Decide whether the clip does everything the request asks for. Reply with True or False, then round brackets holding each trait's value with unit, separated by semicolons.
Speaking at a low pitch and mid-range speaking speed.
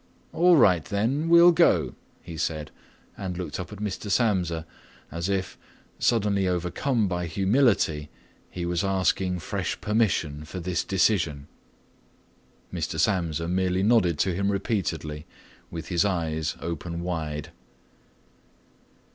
False (90 Hz; 120 wpm)